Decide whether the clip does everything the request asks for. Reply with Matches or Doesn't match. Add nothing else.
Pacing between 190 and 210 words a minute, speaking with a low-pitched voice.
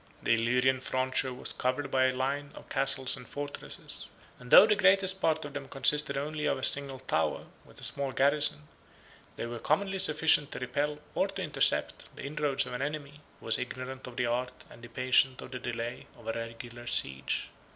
Matches